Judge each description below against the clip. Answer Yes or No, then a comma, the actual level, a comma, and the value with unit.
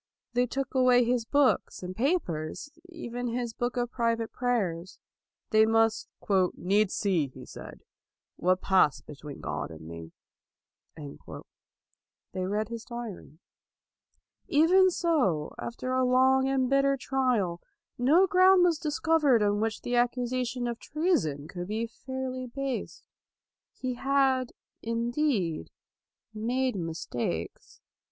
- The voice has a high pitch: Yes, high, 240 Hz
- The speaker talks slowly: Yes, slow, 125 wpm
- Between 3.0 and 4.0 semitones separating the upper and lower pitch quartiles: No, wide, 5.5 semitones